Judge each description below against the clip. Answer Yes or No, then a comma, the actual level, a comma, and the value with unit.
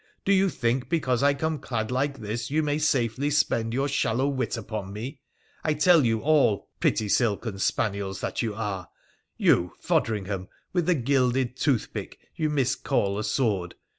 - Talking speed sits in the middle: Yes, average, 165 wpm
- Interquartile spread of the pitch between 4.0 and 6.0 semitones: Yes, average, 4.9 semitones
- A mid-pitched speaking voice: No, low, 125 Hz